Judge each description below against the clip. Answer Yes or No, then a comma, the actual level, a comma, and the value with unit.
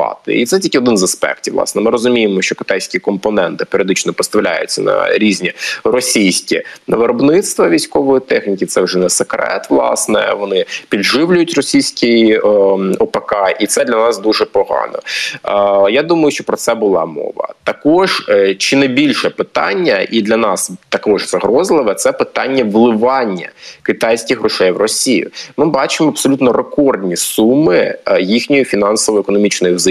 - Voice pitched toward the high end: No, low, 125 Hz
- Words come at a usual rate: Yes, average, 135 wpm